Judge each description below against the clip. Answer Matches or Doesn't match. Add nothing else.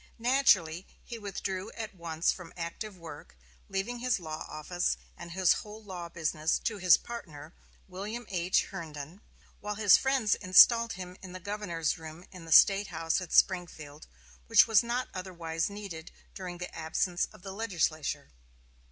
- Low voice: Doesn't match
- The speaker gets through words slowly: Doesn't match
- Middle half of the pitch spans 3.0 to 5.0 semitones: Matches